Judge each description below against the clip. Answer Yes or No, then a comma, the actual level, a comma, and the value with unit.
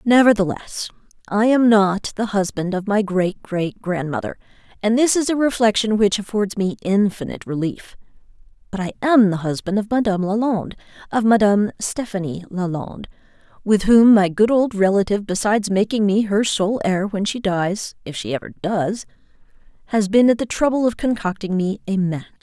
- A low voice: No, high, 205 Hz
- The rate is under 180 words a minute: Yes, average, 155 wpm